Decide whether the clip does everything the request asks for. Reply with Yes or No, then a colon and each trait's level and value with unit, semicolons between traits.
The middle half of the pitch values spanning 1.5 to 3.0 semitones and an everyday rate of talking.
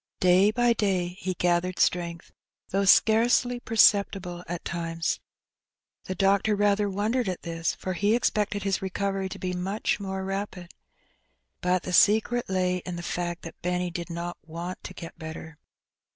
Yes: narrow, 2.6 semitones; average, 160 wpm